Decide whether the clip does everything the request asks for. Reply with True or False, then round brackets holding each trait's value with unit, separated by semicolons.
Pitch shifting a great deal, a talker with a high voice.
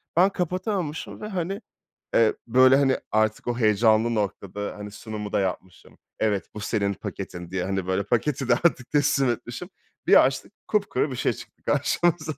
False (6.3 semitones; 115 Hz)